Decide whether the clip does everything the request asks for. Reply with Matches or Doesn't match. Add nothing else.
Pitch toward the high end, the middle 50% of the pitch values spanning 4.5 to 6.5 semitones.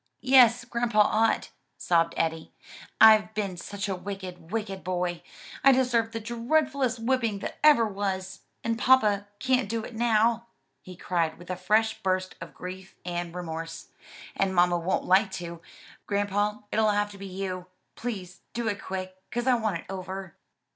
Doesn't match